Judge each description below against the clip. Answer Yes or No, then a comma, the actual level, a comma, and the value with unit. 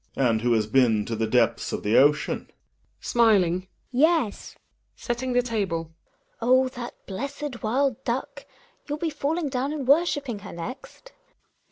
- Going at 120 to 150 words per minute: No, average, 170 wpm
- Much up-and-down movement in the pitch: Yes, wide, 8.9 semitones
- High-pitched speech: Yes, high, 240 Hz